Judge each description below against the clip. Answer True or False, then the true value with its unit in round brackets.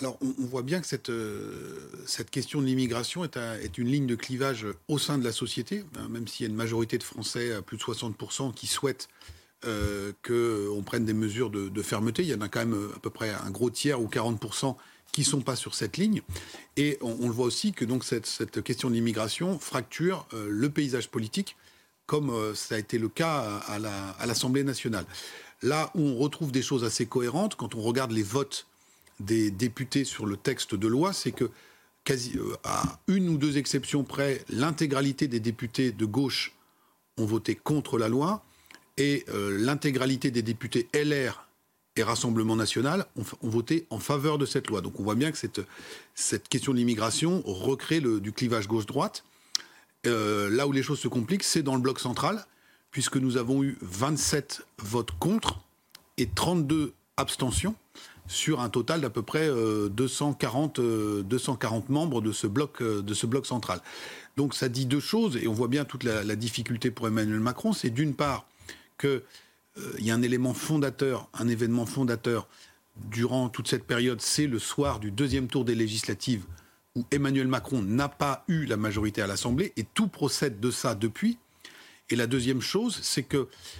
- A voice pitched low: True (125 Hz)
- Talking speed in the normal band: True (190 wpm)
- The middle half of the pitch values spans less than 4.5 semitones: True (3.9 semitones)